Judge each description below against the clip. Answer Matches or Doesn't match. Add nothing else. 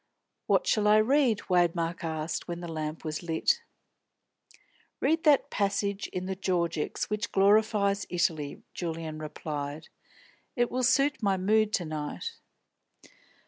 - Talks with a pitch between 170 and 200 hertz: Matches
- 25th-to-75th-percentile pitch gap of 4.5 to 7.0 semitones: Matches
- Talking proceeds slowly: Matches